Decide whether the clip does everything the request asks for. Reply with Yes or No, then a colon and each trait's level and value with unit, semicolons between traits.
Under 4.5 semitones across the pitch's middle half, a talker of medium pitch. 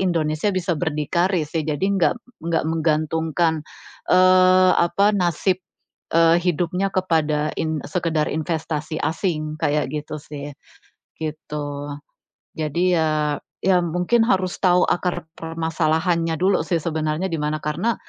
Yes: average, 2.8 semitones; medium, 165 Hz